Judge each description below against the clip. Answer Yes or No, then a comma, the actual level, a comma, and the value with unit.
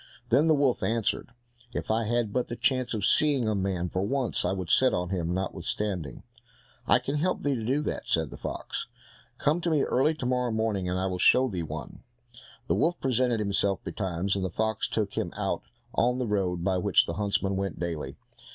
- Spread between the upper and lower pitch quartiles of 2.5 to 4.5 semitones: No, average, 5.3 semitones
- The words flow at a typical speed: No, fast, 210 wpm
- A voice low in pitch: Yes, low, 105 Hz